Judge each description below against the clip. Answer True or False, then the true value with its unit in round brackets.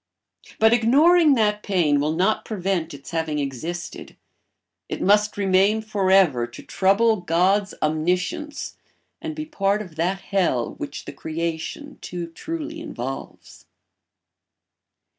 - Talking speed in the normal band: False (125 wpm)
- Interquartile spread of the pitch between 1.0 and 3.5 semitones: False (5.1 semitones)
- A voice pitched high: True (195 Hz)